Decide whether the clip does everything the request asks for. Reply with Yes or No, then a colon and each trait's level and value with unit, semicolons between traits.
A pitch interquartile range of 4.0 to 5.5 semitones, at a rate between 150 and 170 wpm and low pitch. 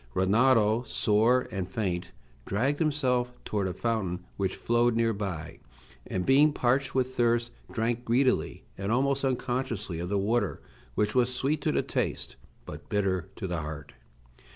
Yes: average, 4.7 semitones; average, 155 wpm; low, 115 Hz